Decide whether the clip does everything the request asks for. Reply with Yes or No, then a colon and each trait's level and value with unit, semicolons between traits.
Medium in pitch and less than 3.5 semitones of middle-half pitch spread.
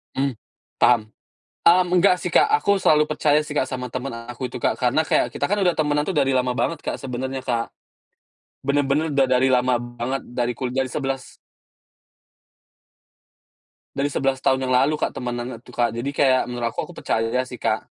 No: low, 130 Hz; average, 2.9 semitones